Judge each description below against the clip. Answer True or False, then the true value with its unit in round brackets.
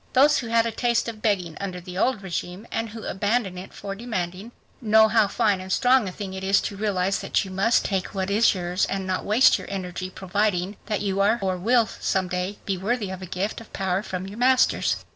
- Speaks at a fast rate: True (230 wpm)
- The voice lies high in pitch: True (200 Hz)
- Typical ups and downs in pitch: True (3.0 semitones)